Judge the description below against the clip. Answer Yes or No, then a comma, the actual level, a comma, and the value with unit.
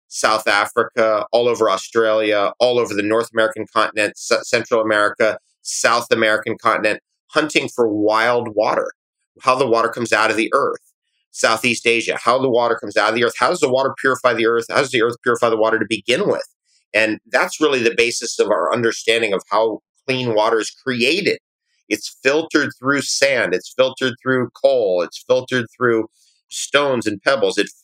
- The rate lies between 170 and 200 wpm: Yes, average, 185 wpm